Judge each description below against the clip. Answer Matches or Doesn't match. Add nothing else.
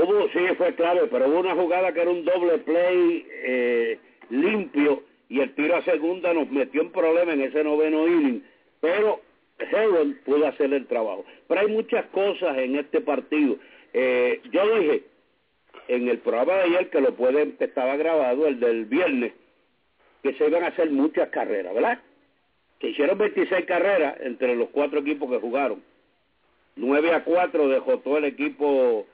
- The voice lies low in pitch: Doesn't match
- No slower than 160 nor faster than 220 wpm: Matches